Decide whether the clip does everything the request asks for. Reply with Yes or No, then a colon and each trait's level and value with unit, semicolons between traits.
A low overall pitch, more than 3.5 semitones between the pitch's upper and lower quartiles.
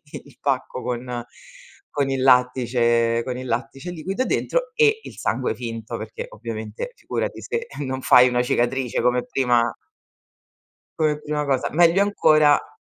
Yes: low, 130 Hz; average, 4.1 semitones